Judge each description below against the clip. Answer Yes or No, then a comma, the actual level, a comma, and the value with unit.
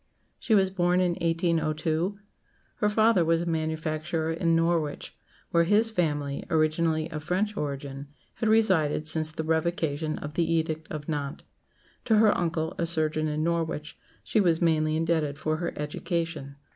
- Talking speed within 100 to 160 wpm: Yes, average, 155 wpm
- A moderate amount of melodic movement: No, narrow, 1.9 semitones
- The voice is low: No, medium, 160 Hz